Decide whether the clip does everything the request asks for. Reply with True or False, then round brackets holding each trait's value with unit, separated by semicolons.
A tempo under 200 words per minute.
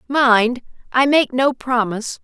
True (135 wpm)